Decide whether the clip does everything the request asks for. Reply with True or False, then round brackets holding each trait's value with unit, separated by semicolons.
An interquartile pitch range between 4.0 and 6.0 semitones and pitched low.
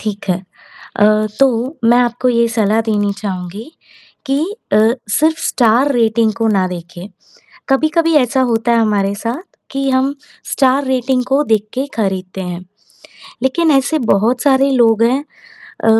False (4.4 semitones; 235 Hz)